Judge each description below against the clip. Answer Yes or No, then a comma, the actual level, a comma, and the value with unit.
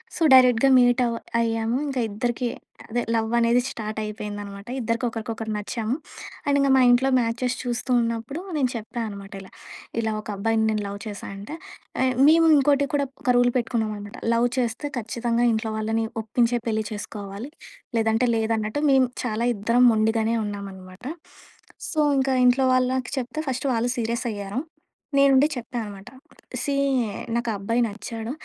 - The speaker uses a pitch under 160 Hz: No, high, 230 Hz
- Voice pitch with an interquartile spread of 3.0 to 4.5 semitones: No, narrow, 2.4 semitones